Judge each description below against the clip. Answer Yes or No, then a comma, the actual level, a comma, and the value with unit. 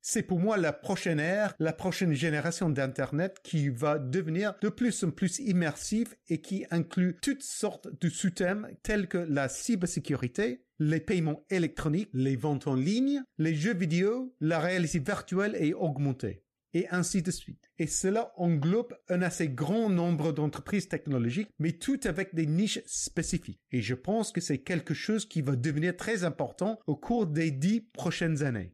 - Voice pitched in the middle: Yes, medium, 175 Hz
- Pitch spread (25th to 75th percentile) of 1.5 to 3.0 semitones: No, average, 4.8 semitones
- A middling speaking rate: Yes, average, 170 wpm